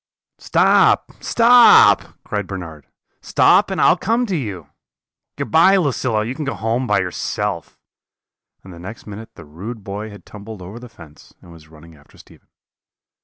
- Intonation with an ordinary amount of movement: No, wide, 6.2 semitones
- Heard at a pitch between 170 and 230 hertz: No, low, 105 Hz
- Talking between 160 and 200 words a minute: Yes, average, 170 wpm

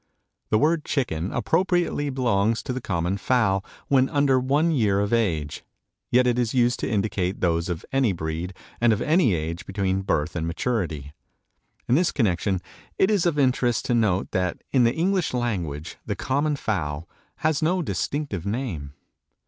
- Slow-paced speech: No, average, 165 wpm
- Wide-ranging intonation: Yes, wide, 7.0 semitones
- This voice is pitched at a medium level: No, low, 115 Hz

